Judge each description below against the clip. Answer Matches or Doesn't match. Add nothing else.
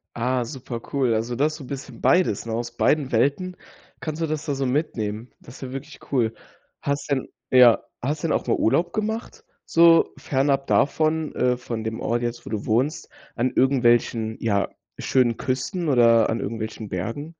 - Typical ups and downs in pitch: Matches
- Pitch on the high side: Doesn't match